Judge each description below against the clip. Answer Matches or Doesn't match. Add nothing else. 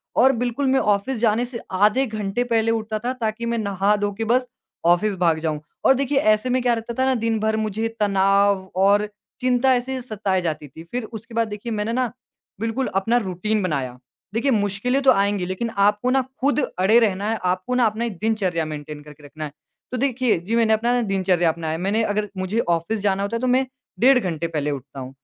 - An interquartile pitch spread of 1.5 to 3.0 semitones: Doesn't match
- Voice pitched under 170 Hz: Doesn't match